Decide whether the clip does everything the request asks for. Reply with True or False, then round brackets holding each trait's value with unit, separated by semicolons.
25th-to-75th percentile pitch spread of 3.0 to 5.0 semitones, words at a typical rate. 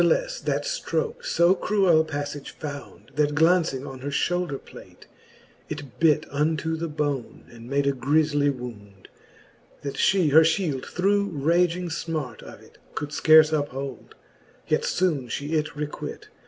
True (3.5 semitones; 150 wpm)